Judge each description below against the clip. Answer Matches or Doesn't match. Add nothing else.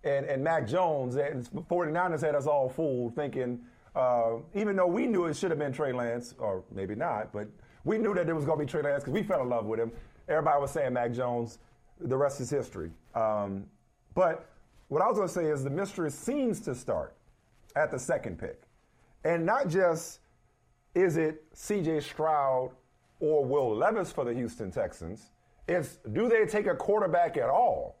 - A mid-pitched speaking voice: Matches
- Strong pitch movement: Matches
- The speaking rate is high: Doesn't match